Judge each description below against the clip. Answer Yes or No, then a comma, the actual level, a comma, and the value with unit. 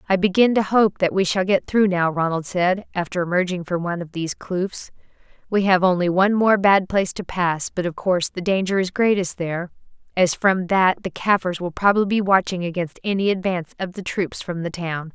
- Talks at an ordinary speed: No, fast, 215 wpm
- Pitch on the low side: No, medium, 185 Hz